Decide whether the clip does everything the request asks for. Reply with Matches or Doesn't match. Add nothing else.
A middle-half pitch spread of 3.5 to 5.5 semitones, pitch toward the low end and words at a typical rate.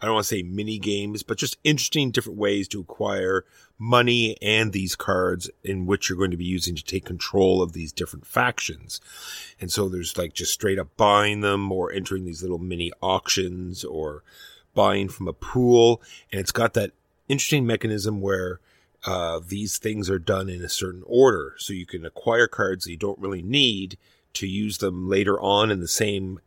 Doesn't match